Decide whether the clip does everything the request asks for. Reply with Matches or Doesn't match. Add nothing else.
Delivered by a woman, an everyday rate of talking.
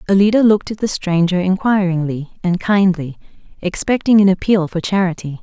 Matches